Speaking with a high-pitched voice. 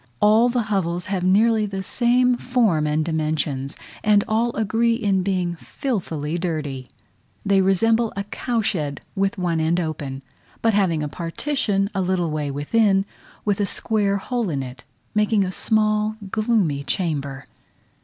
Yes: high, 195 Hz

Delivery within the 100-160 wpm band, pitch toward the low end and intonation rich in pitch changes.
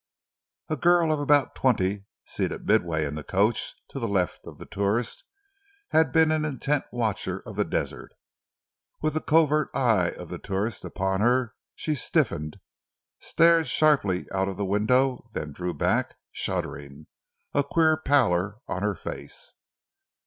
Yes: average, 150 wpm; low, 115 Hz; wide, 7.8 semitones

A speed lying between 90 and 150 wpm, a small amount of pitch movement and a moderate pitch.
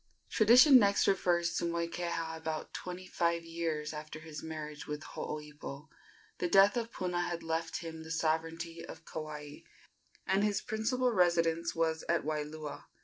Yes: average, 145 wpm; narrow, 2.2 semitones; medium, 165 Hz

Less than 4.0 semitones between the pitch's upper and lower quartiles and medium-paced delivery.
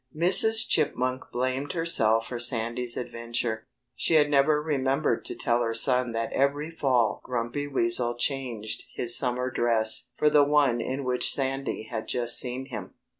Yes: average, 3.0 semitones; average, 155 wpm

